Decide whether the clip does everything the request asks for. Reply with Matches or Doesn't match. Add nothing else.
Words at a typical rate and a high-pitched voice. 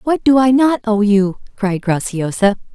Matches